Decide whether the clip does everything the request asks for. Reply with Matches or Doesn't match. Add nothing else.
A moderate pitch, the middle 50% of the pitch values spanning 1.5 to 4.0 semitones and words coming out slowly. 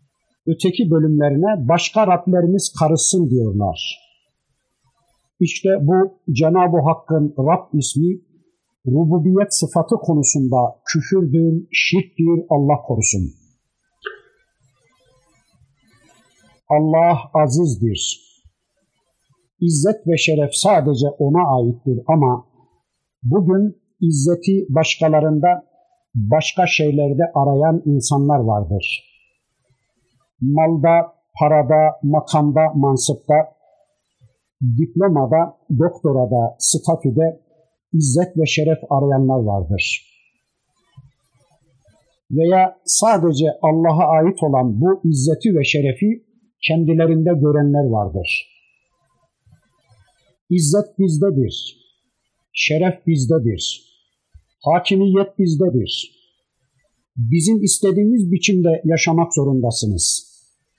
Doesn't match